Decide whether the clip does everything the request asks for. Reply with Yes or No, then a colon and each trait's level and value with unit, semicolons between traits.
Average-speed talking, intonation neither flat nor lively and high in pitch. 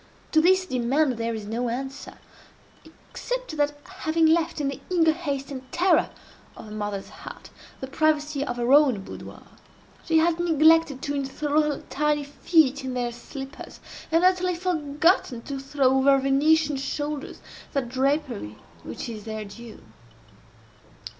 Yes: average, 145 wpm; average, 3.8 semitones; very high, 285 Hz